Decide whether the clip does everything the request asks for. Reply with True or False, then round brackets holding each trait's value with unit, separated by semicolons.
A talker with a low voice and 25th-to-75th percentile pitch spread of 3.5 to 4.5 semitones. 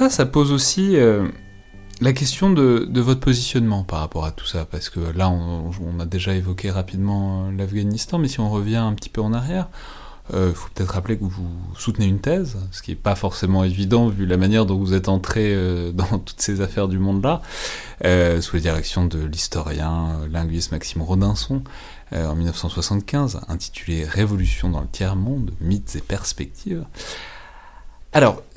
True (95 Hz; 3.8 semitones)